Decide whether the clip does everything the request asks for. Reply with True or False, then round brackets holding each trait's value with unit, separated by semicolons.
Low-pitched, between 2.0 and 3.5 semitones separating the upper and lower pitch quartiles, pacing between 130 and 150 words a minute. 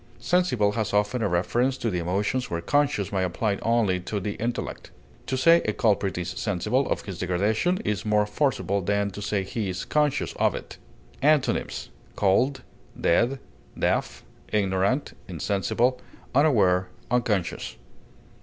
False (105 Hz; 4.8 semitones; 145 wpm)